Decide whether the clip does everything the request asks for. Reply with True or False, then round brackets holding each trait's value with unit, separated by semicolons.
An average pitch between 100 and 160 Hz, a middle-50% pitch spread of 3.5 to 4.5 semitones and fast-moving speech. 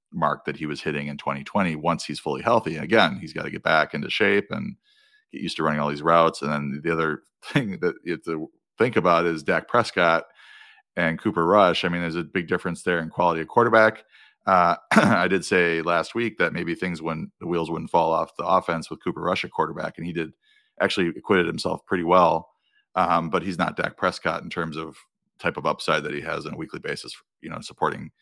False (85 Hz; 3.8 semitones; 230 wpm)